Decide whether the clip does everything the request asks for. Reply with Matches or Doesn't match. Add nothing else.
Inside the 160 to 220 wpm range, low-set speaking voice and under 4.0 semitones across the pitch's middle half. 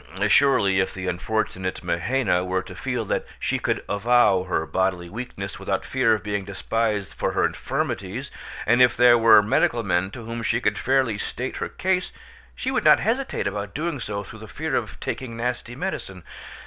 Doesn't match